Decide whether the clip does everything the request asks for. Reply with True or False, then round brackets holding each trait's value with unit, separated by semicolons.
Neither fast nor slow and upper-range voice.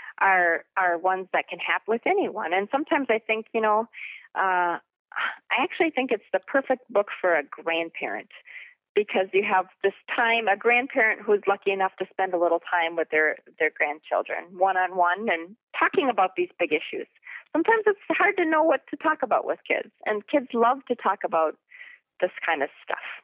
True (190 wpm; 215 Hz)